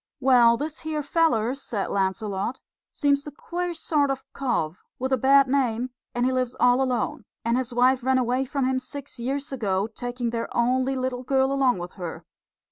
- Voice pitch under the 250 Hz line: No, very high, 255 Hz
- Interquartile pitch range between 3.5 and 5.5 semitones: No, narrow, 2.5 semitones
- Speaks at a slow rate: No, average, 185 wpm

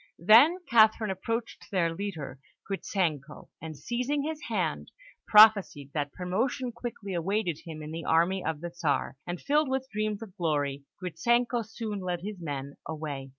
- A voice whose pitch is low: No, high, 190 Hz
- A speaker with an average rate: Yes, average, 150 wpm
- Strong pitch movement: Yes, wide, 6.0 semitones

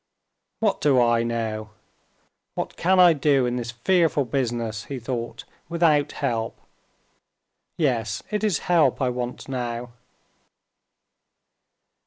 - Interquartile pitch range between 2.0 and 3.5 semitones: No, average, 4.5 semitones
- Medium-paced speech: No, slow, 115 wpm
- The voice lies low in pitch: Yes, low, 125 Hz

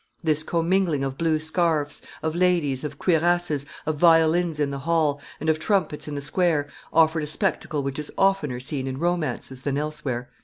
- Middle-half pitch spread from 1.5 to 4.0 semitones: Yes, average, 2.8 semitones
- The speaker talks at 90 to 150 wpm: No, average, 180 wpm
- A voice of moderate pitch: Yes, medium, 155 Hz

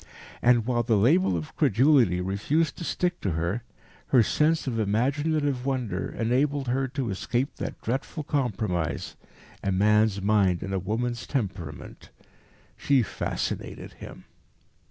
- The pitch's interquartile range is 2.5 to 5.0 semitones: No, wide, 5.6 semitones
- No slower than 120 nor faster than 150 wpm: Yes, slow, 135 wpm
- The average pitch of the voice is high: No, low, 120 Hz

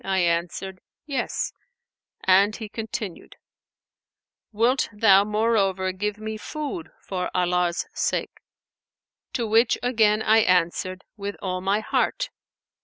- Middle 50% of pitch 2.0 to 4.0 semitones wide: Yes, average, 3.0 semitones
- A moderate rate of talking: No, slow, 110 wpm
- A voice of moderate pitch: No, high, 205 Hz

